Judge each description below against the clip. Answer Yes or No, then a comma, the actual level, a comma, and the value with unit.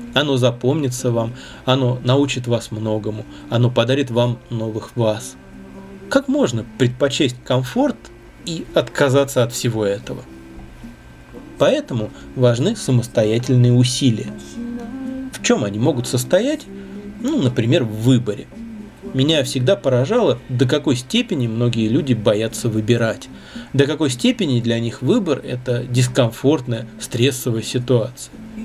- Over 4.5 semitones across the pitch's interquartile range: No, average, 3.5 semitones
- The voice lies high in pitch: No, low, 125 Hz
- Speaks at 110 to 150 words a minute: Yes, average, 115 wpm